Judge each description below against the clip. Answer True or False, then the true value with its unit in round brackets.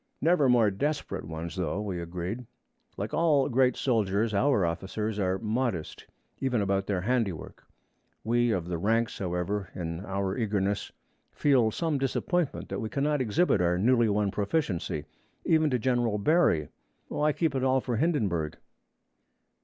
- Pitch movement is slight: False (5.6 semitones)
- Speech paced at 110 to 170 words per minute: True (145 wpm)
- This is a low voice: True (110 Hz)